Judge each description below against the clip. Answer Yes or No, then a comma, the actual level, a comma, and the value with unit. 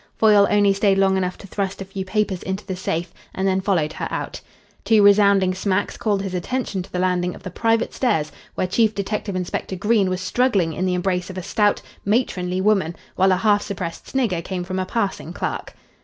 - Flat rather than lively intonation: Yes, narrow, 2.0 semitones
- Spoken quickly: Yes, fast, 210 wpm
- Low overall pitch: No, high, 190 Hz